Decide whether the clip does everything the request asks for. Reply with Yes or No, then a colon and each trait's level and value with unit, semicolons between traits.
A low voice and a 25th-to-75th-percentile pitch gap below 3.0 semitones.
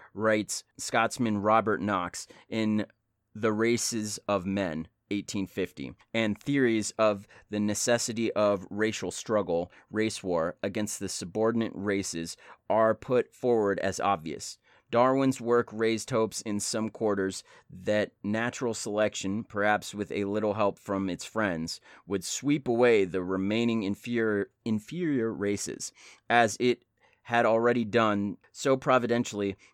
Yes: low, 105 Hz; narrow, 2.4 semitones